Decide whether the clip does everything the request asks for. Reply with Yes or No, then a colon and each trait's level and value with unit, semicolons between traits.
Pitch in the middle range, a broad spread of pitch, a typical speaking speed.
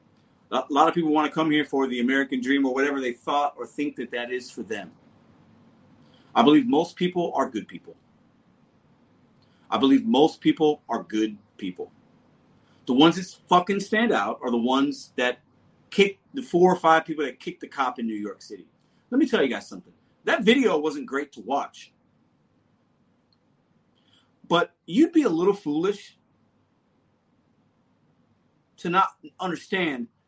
Yes: medium, 155 Hz; wide, 6.5 semitones; average, 165 wpm